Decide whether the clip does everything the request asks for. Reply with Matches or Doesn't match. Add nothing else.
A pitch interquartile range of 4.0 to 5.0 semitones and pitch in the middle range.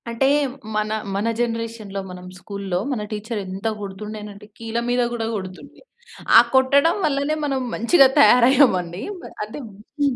Doesn't match